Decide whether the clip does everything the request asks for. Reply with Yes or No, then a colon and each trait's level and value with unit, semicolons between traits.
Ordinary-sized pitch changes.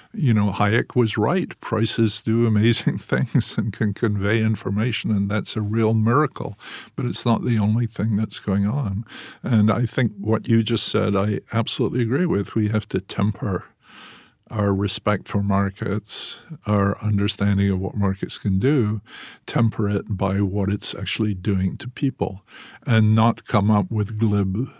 No: narrow, 2.2 semitones